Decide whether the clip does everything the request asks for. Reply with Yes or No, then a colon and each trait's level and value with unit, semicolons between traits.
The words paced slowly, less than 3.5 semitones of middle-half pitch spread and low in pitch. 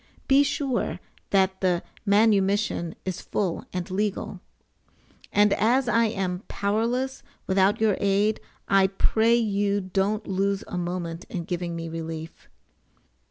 No: slow, 125 wpm; average, 2.9 semitones; high, 195 Hz